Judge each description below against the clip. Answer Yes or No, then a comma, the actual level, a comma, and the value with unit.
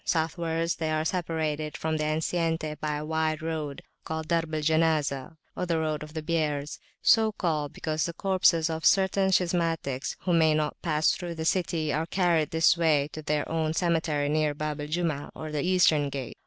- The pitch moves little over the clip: Yes, narrow, 1.6 semitones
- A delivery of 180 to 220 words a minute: Yes, average, 185 wpm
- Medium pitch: Yes, medium, 160 Hz